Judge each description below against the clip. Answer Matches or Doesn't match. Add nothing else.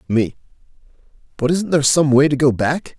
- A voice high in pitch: Doesn't match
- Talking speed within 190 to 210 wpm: Doesn't match